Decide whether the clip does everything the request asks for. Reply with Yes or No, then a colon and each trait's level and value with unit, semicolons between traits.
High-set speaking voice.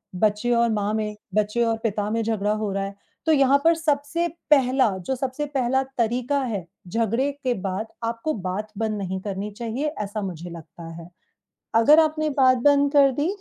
Yes: high, 230 Hz